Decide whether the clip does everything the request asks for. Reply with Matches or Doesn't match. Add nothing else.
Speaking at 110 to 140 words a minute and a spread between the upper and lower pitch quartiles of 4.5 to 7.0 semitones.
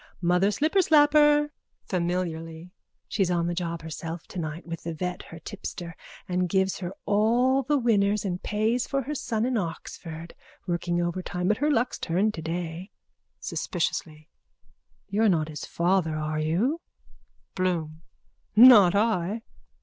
Matches